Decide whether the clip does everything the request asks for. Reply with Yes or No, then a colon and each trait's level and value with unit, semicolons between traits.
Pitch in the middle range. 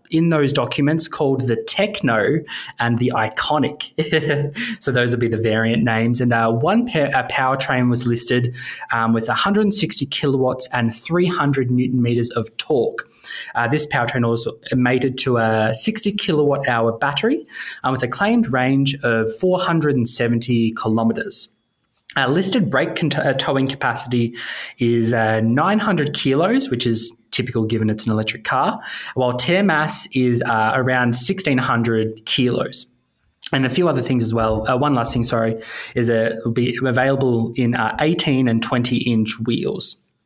No: low, 125 Hz